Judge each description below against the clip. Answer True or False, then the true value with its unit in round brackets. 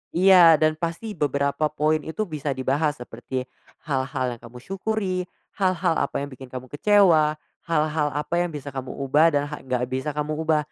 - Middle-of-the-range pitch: True (150 Hz)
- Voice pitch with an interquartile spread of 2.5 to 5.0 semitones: True (3.3 semitones)